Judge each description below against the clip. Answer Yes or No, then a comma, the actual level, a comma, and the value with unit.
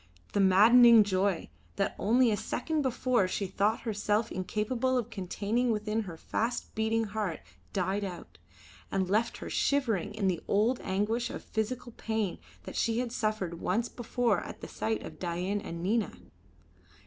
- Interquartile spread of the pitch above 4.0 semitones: No, average, 3.3 semitones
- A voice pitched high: Yes, high, 215 Hz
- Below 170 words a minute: Yes, average, 160 wpm